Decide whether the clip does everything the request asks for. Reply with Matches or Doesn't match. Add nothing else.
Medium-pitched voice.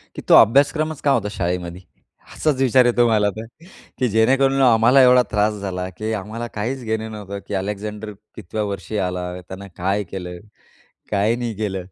Doesn't match